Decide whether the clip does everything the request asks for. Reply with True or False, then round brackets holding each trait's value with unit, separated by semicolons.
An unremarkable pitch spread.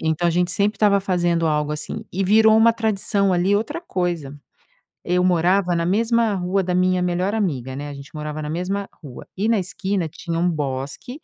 True (3.7 semitones)